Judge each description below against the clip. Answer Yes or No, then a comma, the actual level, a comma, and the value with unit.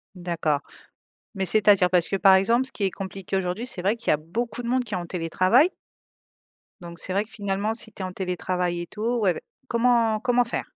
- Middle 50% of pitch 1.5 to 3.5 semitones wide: No, average, 4.2 semitones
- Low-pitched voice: No, high, 195 Hz